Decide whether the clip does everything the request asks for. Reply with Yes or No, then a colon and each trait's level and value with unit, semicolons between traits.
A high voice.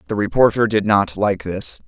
No: low, 105 Hz